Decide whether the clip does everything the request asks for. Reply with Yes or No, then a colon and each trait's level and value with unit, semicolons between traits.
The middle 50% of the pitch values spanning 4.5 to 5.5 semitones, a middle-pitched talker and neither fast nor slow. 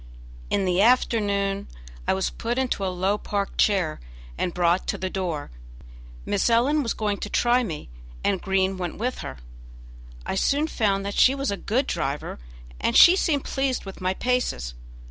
No: average, 4.8 semitones; high, 200 Hz; average, 175 wpm